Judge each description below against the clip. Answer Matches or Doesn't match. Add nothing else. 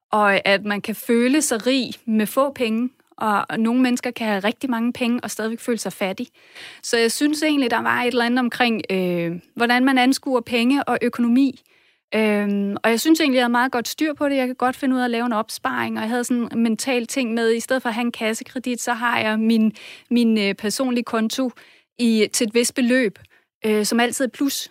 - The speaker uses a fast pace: Matches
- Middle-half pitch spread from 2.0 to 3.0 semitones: Matches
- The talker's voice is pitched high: Matches